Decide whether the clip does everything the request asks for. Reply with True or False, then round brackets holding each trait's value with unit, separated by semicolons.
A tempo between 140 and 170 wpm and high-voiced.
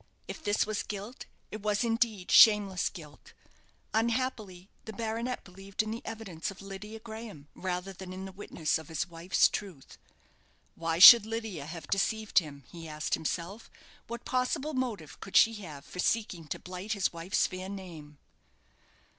True (160 wpm; 195 Hz)